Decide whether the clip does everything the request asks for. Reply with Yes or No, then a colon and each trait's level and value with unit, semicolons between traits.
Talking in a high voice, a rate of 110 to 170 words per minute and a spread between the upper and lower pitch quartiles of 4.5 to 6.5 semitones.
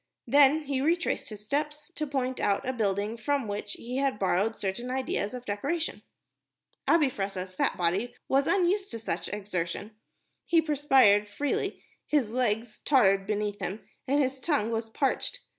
Yes: high, 245 Hz; average, 160 wpm; wide, 5.6 semitones